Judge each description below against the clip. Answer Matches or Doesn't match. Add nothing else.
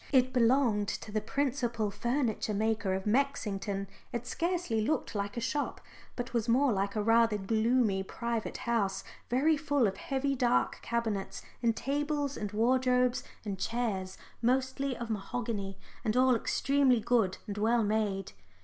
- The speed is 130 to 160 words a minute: Matches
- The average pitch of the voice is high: Matches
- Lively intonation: Doesn't match